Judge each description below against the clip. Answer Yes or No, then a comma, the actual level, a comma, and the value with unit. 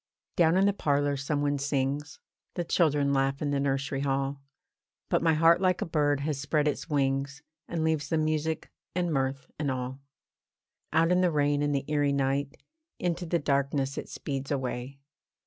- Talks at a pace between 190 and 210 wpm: No, average, 180 wpm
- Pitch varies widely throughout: No, narrow, 2.4 semitones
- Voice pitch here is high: No, medium, 145 Hz